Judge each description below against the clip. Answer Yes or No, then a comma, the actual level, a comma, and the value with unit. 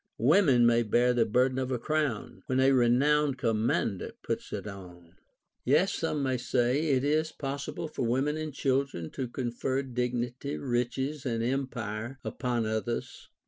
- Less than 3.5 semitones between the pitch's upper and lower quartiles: Yes, average, 2.7 semitones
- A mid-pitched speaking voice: No, low, 125 Hz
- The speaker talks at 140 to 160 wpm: Yes, average, 155 wpm